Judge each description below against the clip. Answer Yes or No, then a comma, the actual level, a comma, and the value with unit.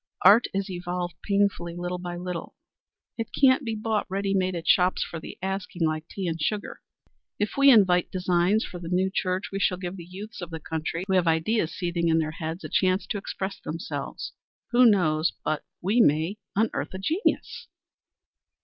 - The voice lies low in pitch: No, medium, 185 Hz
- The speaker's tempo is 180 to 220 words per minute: Yes, average, 185 wpm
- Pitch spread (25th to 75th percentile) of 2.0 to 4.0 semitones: Yes, average, 2.8 semitones